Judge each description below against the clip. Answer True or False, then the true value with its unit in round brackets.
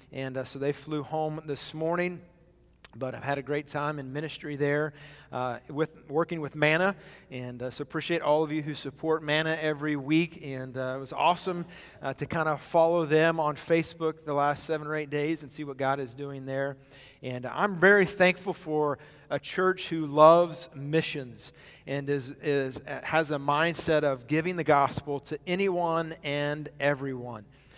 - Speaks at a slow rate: False (180 wpm)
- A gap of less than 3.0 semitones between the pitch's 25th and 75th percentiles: True (2.4 semitones)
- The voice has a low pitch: False (150 Hz)